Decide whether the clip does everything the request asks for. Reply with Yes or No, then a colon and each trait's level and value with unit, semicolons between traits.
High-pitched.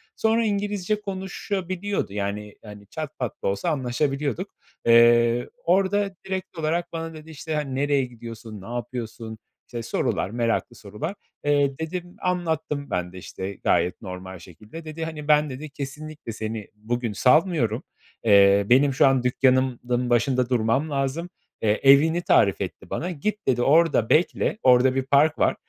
No: low, 135 Hz